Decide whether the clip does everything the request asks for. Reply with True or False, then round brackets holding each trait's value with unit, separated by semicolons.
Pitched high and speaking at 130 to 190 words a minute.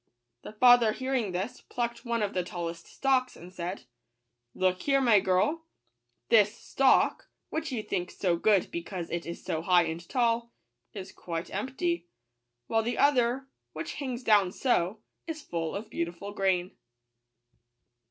True (210 Hz; 150 wpm)